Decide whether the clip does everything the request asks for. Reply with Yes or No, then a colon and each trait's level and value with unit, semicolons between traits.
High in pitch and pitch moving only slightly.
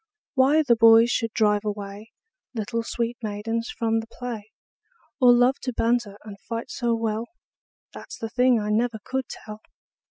Yes: high, 230 Hz; narrow, 2.1 semitones